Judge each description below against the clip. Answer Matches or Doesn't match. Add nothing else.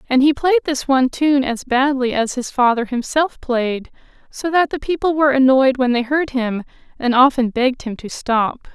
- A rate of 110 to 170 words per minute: Doesn't match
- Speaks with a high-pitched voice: Matches